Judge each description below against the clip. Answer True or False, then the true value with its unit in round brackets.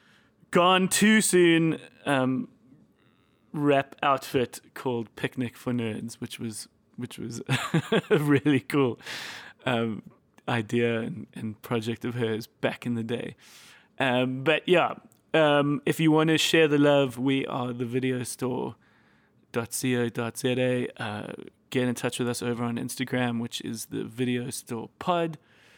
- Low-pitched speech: True (125 Hz)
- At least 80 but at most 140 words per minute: True (135 wpm)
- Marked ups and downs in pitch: False (3.8 semitones)